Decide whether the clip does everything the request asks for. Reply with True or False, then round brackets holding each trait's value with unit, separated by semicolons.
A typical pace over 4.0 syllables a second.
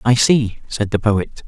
False (3.9 syllables/s)